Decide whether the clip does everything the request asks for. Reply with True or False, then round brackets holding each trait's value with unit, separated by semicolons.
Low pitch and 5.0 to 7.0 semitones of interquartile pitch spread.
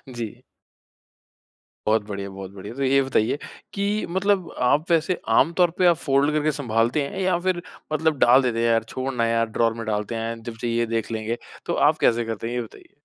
True (120 Hz; 5.3 semitones)